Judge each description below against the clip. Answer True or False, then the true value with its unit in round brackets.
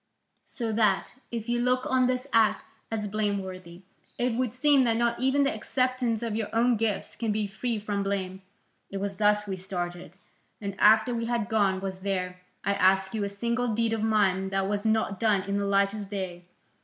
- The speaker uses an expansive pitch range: False (3.1 semitones)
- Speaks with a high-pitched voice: True (210 Hz)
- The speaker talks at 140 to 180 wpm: False (200 wpm)